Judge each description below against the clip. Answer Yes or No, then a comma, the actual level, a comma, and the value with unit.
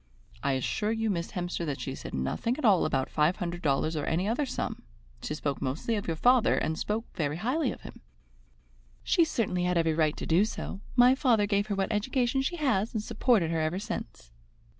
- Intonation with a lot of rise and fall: Yes, wide, 6.3 semitones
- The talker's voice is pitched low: No, high, 190 Hz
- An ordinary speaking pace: No, fast, 215 wpm